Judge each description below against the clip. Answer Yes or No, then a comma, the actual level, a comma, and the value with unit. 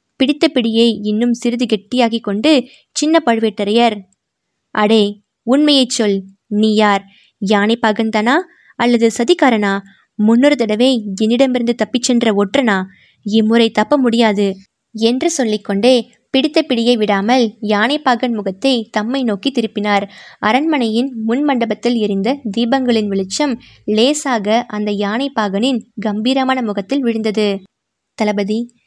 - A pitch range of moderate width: Yes, average, 3.3 semitones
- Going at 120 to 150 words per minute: No, average, 100 wpm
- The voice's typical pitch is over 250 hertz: No, high, 230 Hz